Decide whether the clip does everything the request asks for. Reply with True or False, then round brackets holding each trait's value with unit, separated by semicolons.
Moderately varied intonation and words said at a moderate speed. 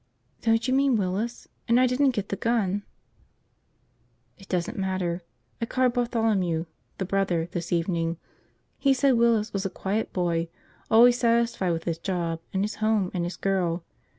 True (4.8 semitones; 160 wpm)